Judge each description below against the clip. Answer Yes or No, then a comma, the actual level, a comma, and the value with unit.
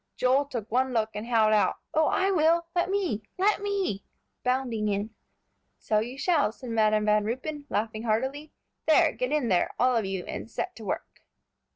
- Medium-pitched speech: No, very high, 250 Hz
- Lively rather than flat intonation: Yes, wide, 6.2 semitones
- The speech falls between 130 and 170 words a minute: No, average, 185 wpm